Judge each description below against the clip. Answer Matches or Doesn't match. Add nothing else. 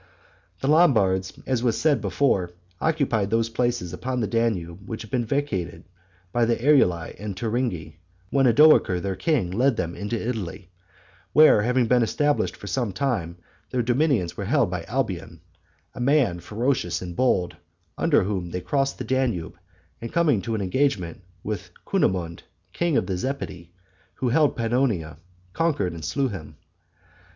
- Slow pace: Doesn't match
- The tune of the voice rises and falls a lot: Matches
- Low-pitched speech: Matches